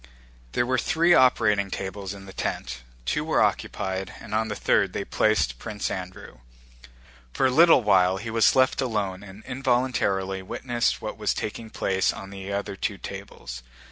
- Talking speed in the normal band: Yes, average, 170 wpm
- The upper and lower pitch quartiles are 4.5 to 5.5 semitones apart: No, average, 3.7 semitones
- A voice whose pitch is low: Yes, low, 100 Hz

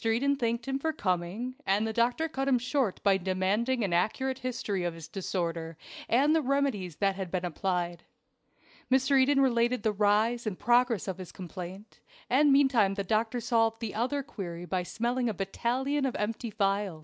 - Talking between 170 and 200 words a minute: Yes, average, 180 wpm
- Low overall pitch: No, high, 225 Hz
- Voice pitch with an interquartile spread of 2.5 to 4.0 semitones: No, average, 5.0 semitones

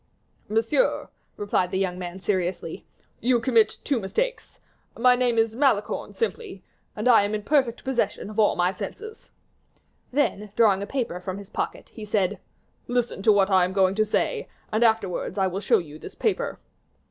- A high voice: Yes, high, 215 Hz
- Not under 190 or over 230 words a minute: No, average, 175 wpm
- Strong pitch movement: No, average, 4.1 semitones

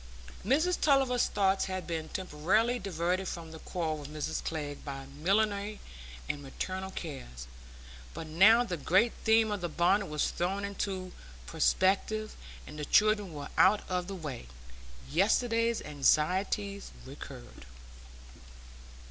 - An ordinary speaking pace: No, slow, 130 wpm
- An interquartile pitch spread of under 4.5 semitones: No, average, 5.1 semitones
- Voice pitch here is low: No, medium, 185 Hz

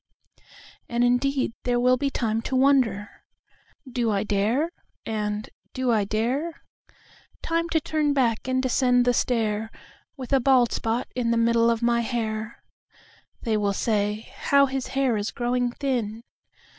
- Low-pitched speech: No, high, 240 Hz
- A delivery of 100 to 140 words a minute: Yes, slow, 135 wpm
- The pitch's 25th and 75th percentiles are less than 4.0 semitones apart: Yes, average, 2.8 semitones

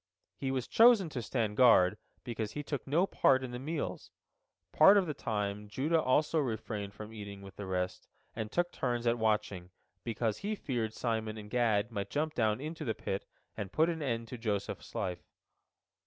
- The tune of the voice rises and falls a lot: Yes, wide, 5.8 semitones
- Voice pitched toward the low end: Yes, low, 115 Hz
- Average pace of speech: Yes, average, 185 wpm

